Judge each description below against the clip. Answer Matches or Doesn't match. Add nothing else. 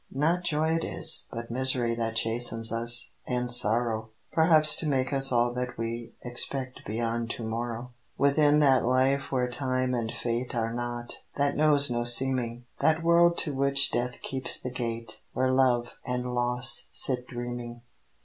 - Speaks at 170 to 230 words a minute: Doesn't match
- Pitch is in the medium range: Doesn't match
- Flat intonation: Matches